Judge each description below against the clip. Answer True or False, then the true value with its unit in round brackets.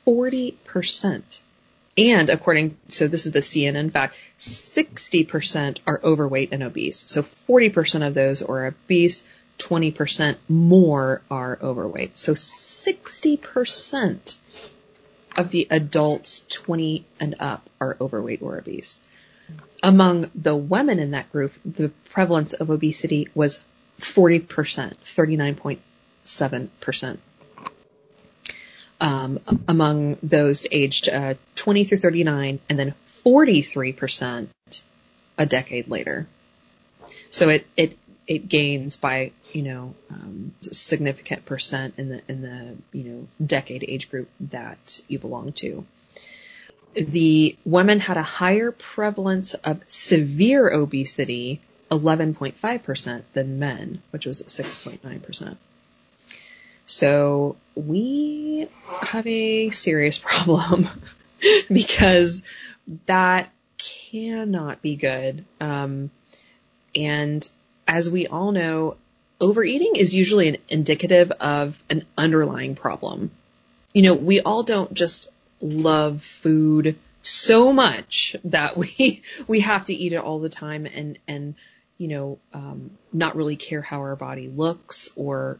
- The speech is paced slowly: True (120 wpm)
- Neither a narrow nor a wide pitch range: True (4.6 semitones)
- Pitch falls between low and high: True (155 Hz)